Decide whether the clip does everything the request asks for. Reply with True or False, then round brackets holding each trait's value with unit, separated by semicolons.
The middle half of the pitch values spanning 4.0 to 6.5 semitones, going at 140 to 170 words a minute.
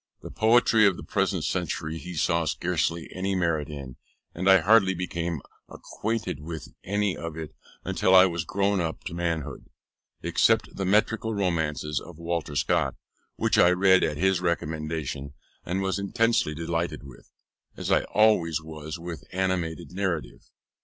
False (3.2 semitones; 155 wpm)